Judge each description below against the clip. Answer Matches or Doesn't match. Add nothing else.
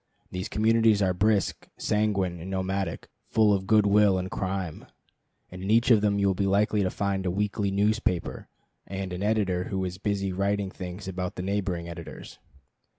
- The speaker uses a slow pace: Doesn't match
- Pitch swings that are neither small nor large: Doesn't match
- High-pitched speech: Doesn't match